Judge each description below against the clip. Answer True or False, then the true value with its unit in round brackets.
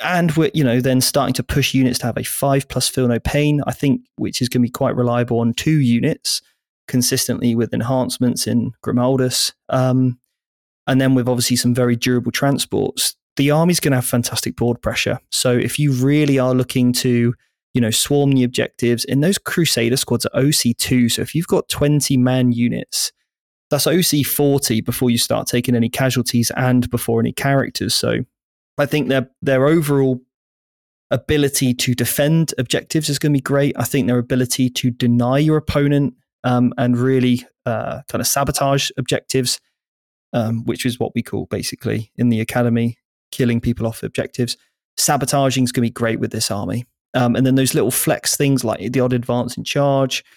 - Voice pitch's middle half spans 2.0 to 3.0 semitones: True (2.4 semitones)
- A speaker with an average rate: True (185 wpm)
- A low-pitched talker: True (125 Hz)